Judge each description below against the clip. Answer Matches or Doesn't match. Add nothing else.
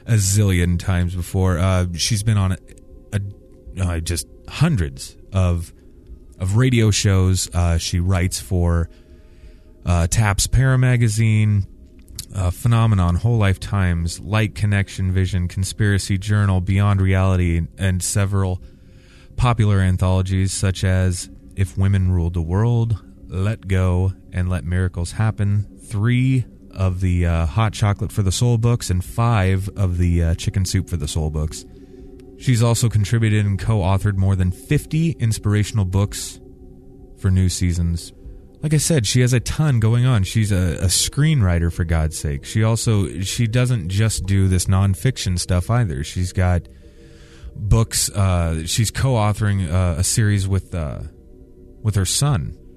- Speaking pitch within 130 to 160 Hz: Doesn't match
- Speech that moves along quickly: Doesn't match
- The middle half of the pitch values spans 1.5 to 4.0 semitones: Matches